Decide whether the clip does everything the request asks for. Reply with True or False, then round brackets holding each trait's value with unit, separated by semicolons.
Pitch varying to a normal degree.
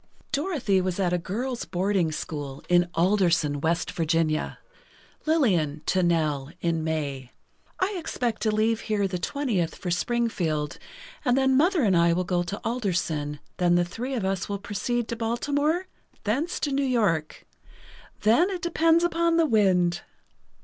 False (7.0 semitones)